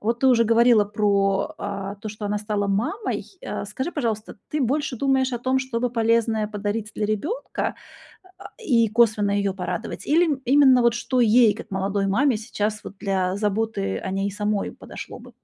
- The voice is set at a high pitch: Yes, high, 220 Hz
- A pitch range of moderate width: Yes, average, 3.5 semitones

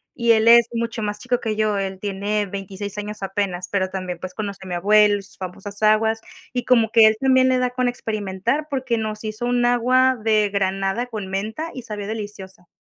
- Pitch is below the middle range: No, high, 215 Hz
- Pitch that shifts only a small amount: No, average, 3.1 semitones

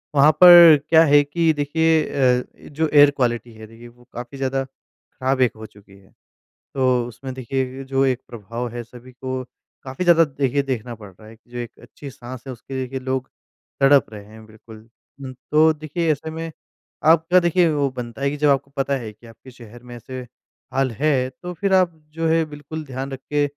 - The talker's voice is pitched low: Yes, low, 130 Hz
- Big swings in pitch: No, average, 3.6 semitones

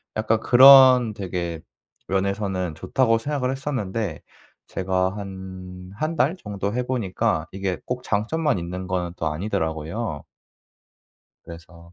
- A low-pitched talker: Yes, low, 100 Hz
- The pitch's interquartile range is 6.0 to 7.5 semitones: No, average, 5.2 semitones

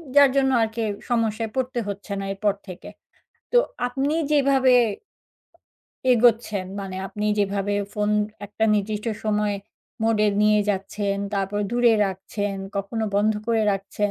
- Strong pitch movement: No, average, 2.8 semitones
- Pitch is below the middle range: No, high, 210 Hz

